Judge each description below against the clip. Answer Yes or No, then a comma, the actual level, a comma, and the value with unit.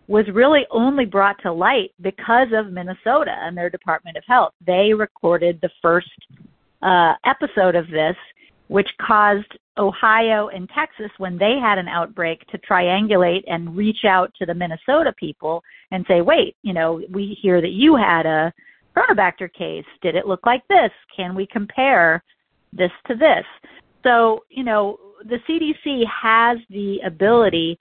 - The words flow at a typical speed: Yes, average, 160 wpm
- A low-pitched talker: No, high, 200 Hz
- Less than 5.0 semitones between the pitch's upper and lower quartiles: Yes, average, 4.3 semitones